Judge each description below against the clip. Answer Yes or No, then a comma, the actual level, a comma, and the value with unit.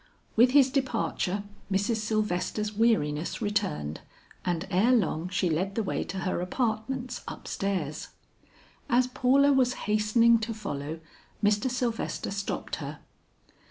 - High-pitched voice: Yes, high, 215 Hz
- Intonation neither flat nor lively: Yes, average, 4.7 semitones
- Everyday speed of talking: No, slow, 125 wpm